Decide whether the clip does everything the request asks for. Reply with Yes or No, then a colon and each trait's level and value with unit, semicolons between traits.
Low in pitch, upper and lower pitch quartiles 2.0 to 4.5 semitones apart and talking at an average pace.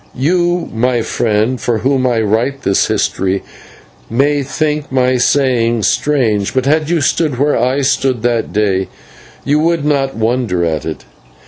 Yes: low, 130 Hz; average, 4.1 semitones; average, 150 wpm